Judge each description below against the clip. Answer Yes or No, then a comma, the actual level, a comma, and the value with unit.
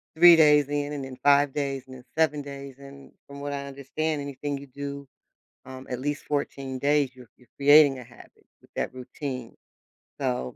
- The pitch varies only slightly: Yes, narrow, 1.7 semitones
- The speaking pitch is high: No, medium, 140 Hz